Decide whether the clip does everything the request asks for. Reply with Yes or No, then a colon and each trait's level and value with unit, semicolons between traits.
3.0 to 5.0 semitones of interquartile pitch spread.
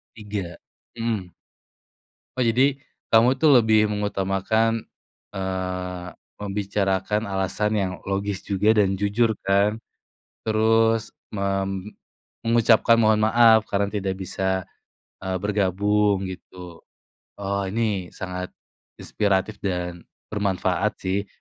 No: narrow, 2.5 semitones